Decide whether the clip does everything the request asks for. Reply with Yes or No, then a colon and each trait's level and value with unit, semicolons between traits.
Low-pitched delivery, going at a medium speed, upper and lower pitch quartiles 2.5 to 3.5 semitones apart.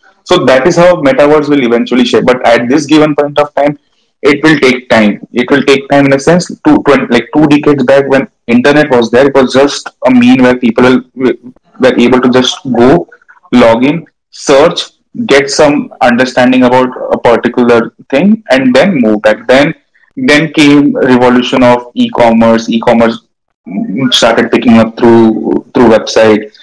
Yes: low, 130 Hz; average, 165 wpm; average, 3.2 semitones